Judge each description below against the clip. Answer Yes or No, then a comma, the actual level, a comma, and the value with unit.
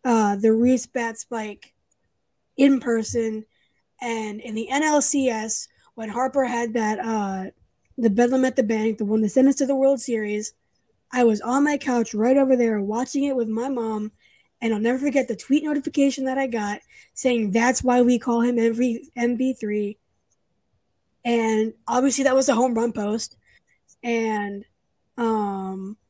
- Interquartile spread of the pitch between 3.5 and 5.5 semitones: No, average, 2.9 semitones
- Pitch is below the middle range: No, high, 235 Hz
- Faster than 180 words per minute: No, average, 165 wpm